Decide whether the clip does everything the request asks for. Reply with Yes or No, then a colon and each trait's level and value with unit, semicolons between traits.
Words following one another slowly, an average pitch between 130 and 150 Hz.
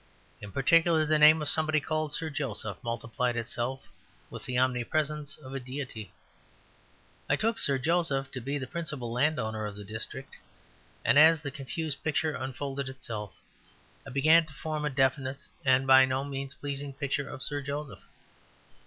No: average, 160 wpm; medium, 140 Hz